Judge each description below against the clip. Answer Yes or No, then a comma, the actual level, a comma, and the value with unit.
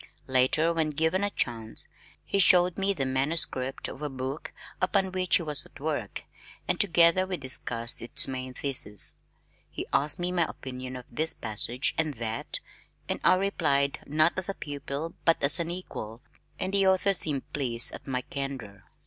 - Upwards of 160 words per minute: Yes, average, 175 wpm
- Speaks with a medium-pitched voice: Yes, medium, 145 Hz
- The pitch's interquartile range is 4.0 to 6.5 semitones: Yes, average, 5.2 semitones